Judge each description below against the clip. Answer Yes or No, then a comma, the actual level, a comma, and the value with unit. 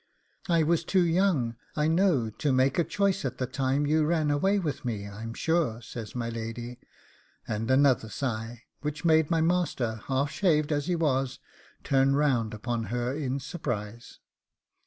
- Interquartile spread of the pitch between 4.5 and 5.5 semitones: Yes, average, 5.2 semitones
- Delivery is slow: No, average, 165 wpm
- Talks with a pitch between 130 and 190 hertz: Yes, low, 135 Hz